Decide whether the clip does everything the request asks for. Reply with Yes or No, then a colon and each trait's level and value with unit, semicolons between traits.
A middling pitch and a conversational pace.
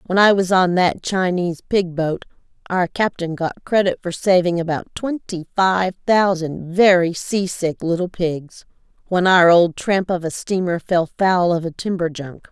Yes: medium, 180 Hz; average, 170 wpm